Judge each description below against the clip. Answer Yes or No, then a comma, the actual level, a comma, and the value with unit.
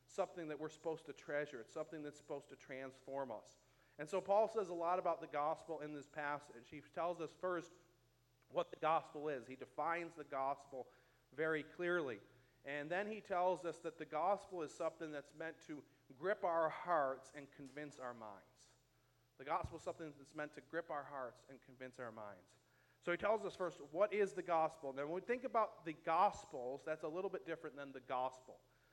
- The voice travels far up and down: No, average, 4.0 semitones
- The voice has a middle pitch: Yes, medium, 155 Hz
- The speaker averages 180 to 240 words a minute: Yes, average, 200 wpm